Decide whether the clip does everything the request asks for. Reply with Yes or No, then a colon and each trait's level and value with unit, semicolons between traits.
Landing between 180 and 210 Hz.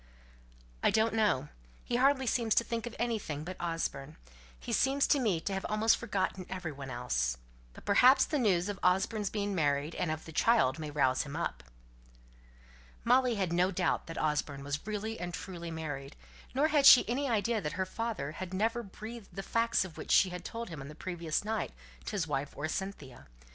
Yes: high, 190 Hz